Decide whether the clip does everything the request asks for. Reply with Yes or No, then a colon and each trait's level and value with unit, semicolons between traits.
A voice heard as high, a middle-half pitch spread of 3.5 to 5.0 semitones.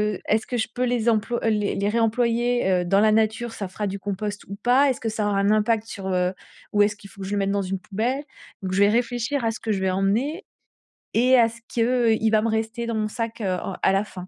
No: high, 215 Hz; average, 2.7 semitones